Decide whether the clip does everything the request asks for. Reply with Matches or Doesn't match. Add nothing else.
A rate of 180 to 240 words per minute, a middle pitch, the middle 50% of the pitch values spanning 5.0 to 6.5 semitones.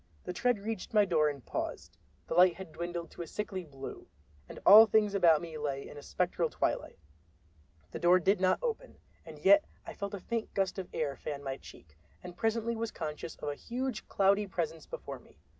Matches